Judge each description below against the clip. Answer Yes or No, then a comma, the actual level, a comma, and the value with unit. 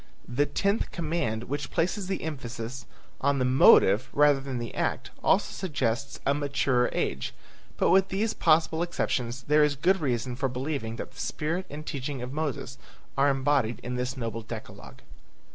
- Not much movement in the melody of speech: No, average, 3.8 semitones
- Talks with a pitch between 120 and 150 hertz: Yes, medium, 140 Hz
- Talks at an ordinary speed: Yes, average, 165 wpm